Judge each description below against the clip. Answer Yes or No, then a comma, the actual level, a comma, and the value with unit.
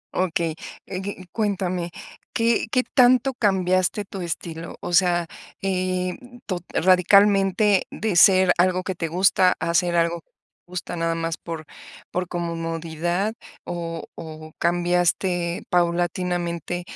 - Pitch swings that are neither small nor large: No, narrow, 1.9 semitones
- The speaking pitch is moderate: Yes, medium, 180 Hz